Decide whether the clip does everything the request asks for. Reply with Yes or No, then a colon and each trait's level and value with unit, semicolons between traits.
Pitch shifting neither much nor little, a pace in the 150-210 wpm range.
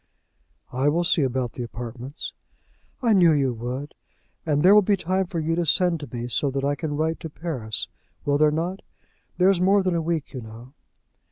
Yes: average, 5.0 semitones; fast, 205 wpm